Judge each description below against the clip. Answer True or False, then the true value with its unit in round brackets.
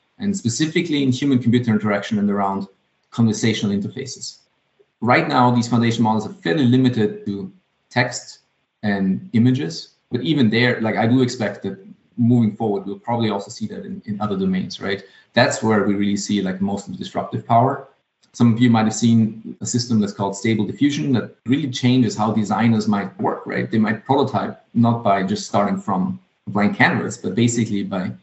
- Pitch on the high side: False (110 Hz)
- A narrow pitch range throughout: False (3.4 semitones)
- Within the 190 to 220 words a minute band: False (180 wpm)